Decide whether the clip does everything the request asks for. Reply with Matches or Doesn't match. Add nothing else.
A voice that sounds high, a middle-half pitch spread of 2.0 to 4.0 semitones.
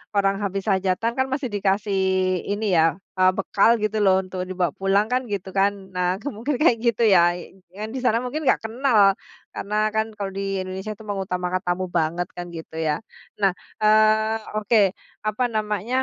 Matches